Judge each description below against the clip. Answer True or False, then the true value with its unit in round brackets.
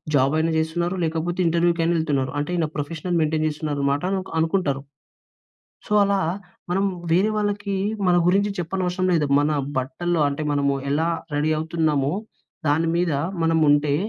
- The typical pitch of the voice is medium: True (160 Hz)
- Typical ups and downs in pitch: True (3.1 semitones)